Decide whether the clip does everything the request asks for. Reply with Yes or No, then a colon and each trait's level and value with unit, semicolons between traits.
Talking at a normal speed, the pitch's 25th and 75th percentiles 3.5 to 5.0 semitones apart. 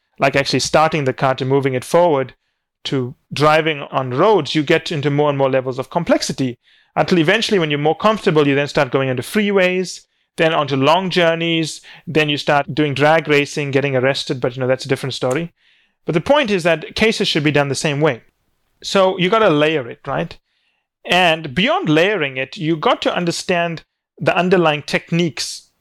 Yes: average, 195 wpm; average, 3.8 semitones